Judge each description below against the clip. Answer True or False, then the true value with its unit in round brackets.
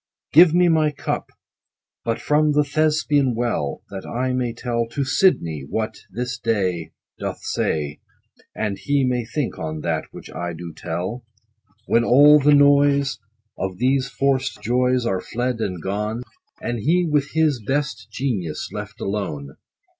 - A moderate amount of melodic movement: False (6.4 semitones)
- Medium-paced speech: True (155 wpm)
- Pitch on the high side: False (125 Hz)